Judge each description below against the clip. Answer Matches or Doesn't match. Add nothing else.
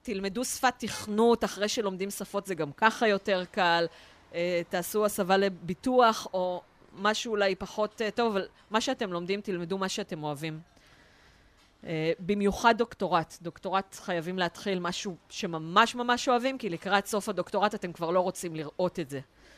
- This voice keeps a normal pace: Doesn't match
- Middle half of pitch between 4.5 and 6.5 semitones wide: Doesn't match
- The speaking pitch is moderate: Doesn't match